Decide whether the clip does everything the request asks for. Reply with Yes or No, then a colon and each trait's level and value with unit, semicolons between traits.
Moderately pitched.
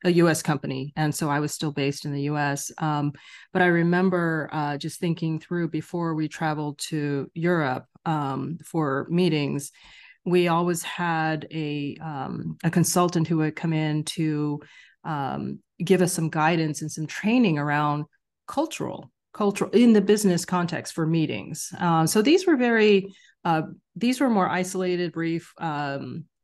Yes: medium, 160 Hz